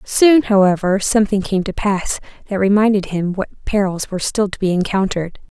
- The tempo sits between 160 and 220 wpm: Yes, average, 170 wpm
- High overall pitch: Yes, high, 200 Hz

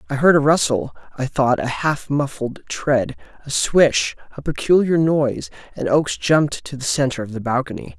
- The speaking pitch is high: No, low, 130 Hz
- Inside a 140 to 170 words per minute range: Yes, average, 165 wpm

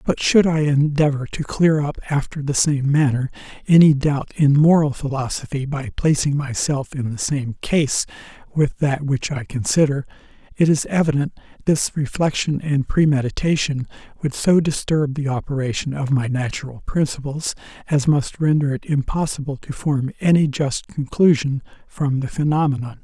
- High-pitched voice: No, medium, 145 Hz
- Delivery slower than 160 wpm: Yes, average, 150 wpm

